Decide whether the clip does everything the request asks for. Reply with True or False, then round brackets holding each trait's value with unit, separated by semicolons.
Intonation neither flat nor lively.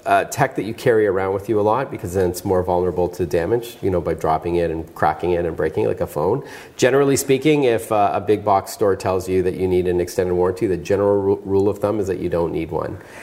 True (4.7 semitones)